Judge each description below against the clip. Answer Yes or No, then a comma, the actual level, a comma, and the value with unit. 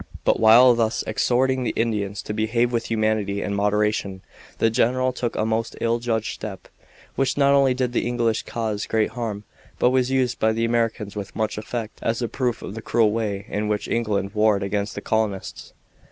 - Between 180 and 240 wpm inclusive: Yes, average, 195 wpm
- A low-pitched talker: Yes, low, 110 Hz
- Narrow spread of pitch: Yes, narrow, 2.3 semitones